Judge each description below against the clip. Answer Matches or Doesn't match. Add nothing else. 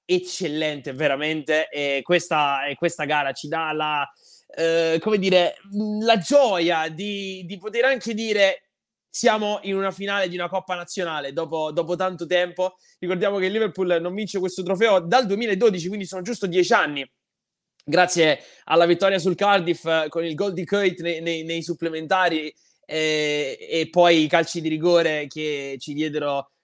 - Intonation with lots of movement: Doesn't match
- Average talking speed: Matches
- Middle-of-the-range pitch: Matches